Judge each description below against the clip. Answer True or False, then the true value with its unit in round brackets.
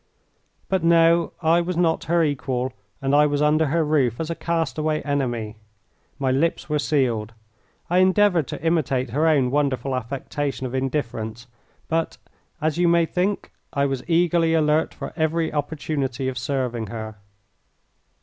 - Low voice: False (150 Hz)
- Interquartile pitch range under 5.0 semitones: True (3.9 semitones)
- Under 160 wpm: True (150 wpm)